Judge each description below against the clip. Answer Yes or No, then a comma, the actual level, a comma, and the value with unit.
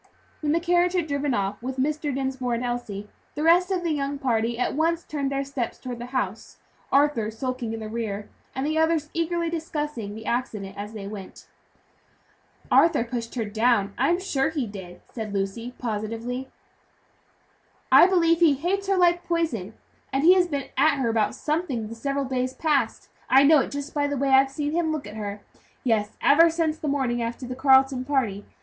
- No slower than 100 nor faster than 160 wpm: No, average, 195 wpm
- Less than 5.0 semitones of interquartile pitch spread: No, wide, 5.4 semitones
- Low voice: No, very high, 265 Hz